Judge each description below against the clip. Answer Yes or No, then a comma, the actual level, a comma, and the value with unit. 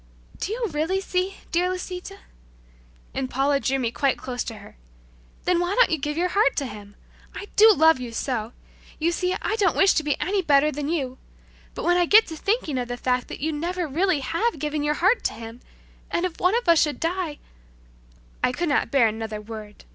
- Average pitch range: No, wide, 6.3 semitones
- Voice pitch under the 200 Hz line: No, very high, 305 Hz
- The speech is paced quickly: Yes, fast, 220 wpm